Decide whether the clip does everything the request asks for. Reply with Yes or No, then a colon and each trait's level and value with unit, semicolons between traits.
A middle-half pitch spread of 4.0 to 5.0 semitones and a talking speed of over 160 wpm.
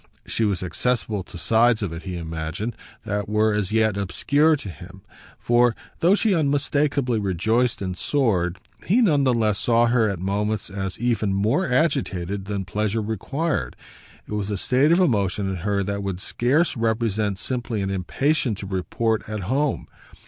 Yes: average, 4.3 semitones; average, 170 wpm